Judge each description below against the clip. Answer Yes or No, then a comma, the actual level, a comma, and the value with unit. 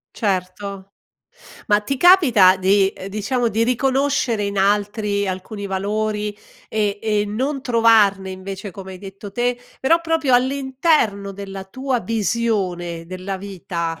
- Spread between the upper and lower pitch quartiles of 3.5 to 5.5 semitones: Yes, average, 3.9 semitones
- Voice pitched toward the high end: Yes, high, 205 Hz